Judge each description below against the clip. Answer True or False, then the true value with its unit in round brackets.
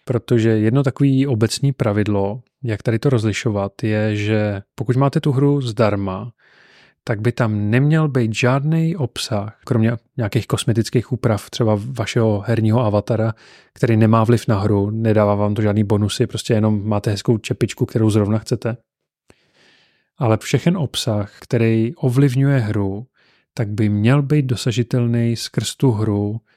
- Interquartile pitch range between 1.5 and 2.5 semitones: False (2.9 semitones)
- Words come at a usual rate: True (140 wpm)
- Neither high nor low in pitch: False (115 Hz)